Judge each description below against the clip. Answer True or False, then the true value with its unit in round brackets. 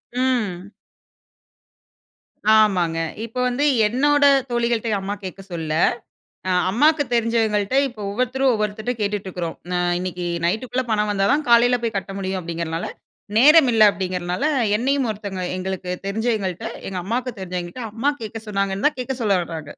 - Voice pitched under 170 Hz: False (210 Hz)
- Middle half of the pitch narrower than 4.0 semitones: False (4.5 semitones)